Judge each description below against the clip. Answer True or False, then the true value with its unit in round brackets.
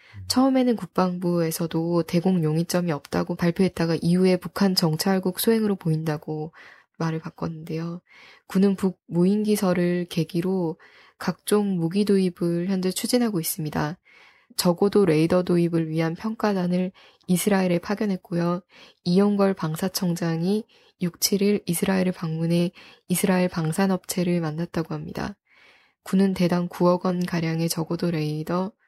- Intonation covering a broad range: False (2.5 semitones)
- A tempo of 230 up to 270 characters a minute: False (310 characters per minute)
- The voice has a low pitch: False (180 Hz)